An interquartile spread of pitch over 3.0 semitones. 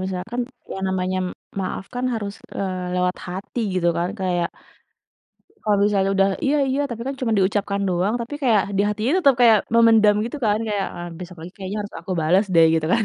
Yes: average, 3.7 semitones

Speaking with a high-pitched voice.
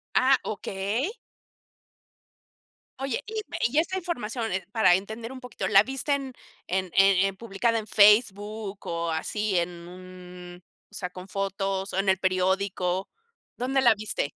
Yes: high, 200 Hz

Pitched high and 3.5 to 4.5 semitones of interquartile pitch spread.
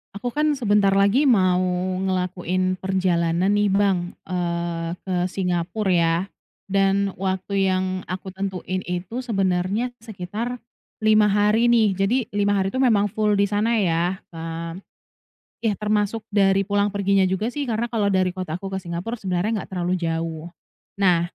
No: high, 195 Hz; narrow, 2.5 semitones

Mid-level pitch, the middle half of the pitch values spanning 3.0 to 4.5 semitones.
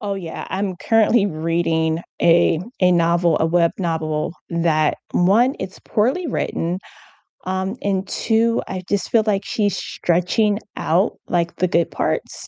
Yes: medium, 180 Hz; average, 3.4 semitones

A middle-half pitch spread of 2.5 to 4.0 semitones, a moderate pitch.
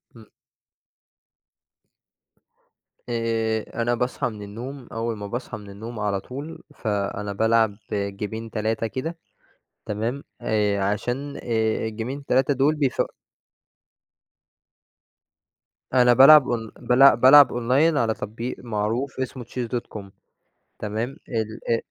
No: average, 3.0 semitones; low, 115 Hz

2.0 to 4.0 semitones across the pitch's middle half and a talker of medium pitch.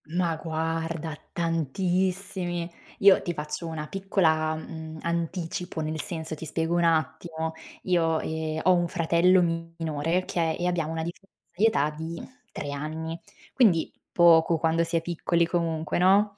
No: narrow, 1.6 semitones; medium, 165 Hz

